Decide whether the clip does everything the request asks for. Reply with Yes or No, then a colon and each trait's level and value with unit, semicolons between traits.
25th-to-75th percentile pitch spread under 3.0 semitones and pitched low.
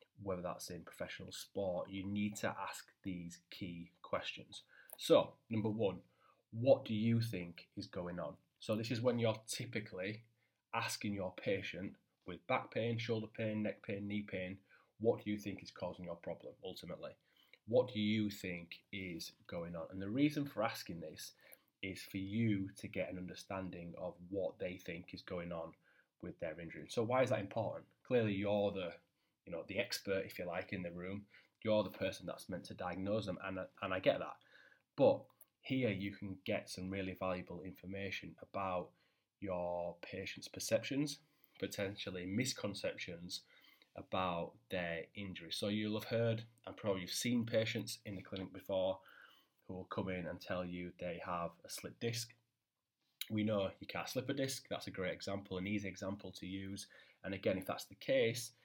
No: average, 3.4 semitones; low, 100 Hz